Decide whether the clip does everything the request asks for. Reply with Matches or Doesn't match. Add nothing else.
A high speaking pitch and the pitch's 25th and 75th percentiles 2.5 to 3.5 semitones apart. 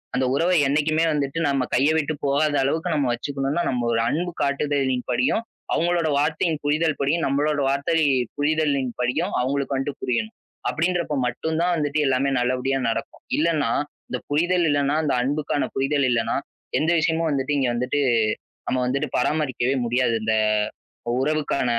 Doesn't match